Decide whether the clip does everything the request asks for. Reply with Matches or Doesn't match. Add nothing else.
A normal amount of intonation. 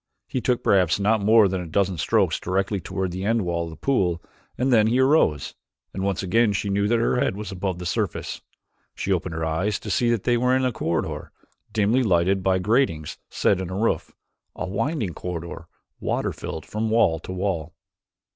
Matches